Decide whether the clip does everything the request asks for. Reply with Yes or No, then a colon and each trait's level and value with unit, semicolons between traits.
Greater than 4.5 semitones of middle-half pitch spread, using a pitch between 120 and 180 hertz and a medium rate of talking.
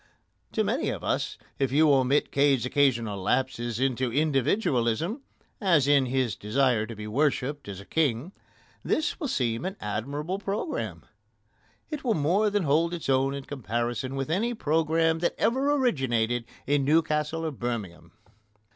Yes: average, 5.1 semitones; medium, 140 Hz; average, 150 wpm